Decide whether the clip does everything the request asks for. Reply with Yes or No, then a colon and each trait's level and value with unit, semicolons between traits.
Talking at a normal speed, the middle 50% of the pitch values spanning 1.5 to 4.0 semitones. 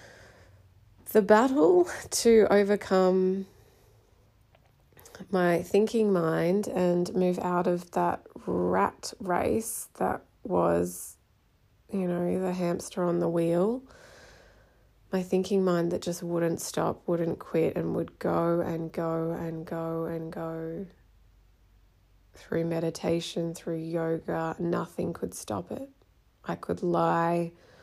No: slow, 110 wpm; narrow, 2.5 semitones